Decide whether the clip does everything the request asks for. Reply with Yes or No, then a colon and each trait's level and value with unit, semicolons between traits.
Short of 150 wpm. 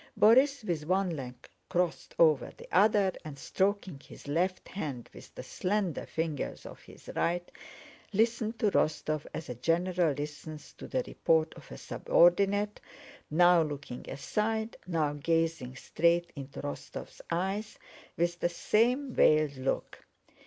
Yes: average, 140 wpm